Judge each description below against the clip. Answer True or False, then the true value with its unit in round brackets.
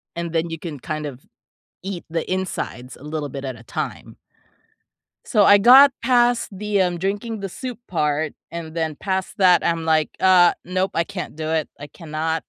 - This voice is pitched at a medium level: True (170 Hz)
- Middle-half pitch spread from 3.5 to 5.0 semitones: True (3.9 semitones)